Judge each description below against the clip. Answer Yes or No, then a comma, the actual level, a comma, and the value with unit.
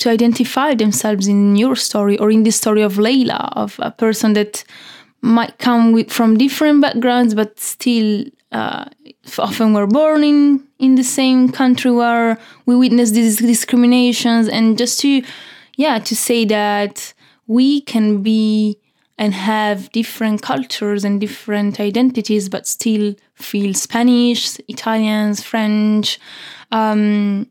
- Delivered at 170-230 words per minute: No, slow, 135 wpm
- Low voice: No, high, 225 Hz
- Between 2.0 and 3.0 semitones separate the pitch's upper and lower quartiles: Yes, average, 2.7 semitones